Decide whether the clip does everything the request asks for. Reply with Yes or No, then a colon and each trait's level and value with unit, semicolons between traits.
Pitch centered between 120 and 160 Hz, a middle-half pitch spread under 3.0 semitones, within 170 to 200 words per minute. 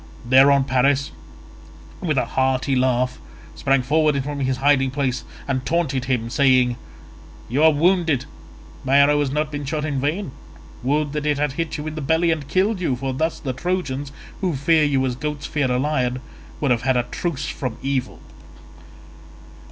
Yes: medium, 140 Hz; narrow, 2.6 semitones; average, 175 wpm